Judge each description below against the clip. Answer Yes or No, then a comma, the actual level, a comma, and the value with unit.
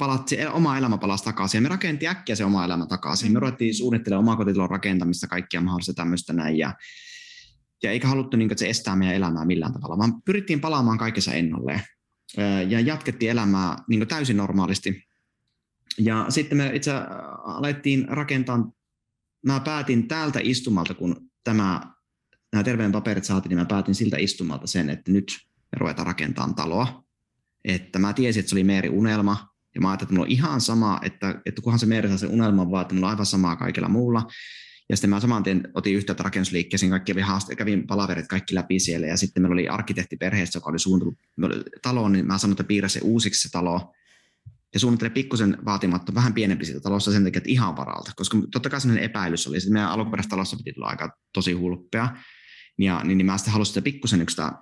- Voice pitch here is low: Yes, low, 100 Hz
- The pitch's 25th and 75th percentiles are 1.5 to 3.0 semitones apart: No, average, 3.8 semitones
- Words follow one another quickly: Yes, fast, 190 wpm